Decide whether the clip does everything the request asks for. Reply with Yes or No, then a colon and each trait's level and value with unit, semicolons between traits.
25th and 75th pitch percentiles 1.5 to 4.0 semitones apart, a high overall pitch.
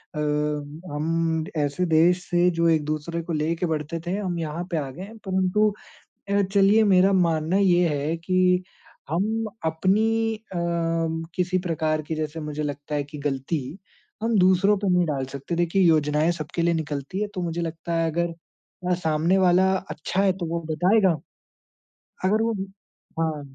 No: average, 3.3 semitones; medium, 170 Hz